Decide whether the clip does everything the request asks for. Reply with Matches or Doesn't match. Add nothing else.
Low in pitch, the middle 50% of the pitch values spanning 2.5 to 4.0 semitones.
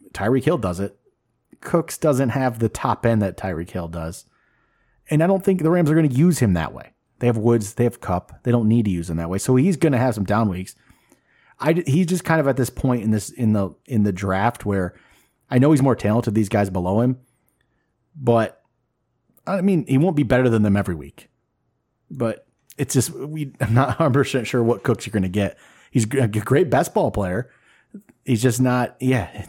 Doesn't match